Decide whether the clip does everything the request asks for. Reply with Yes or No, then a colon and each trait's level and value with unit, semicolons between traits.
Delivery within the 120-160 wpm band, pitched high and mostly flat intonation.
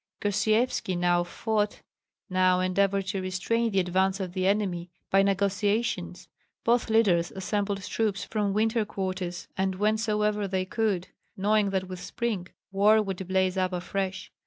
Yes: average, 140 wpm; high, 195 Hz; narrow, 2.3 semitones